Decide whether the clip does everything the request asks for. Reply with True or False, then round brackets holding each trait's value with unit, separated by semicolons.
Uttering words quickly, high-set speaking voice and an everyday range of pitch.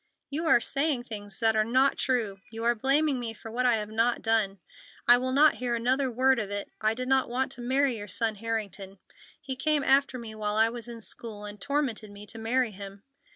True (225 wpm; 235 Hz; 3.3 semitones)